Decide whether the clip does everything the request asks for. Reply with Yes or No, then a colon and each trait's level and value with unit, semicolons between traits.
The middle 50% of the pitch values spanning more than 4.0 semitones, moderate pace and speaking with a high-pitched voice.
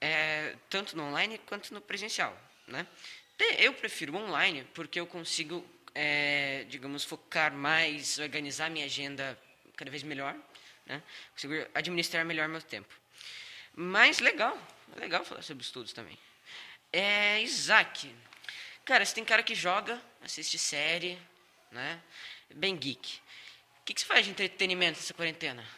No: average, 4.6 semitones; average, 135 wpm; medium, 165 Hz